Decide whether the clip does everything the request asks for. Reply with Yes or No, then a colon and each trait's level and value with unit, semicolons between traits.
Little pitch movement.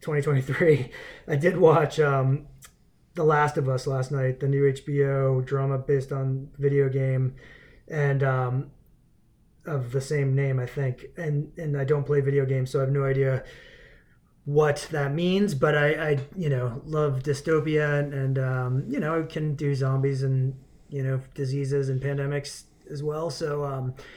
Yes: narrow, 1.8 semitones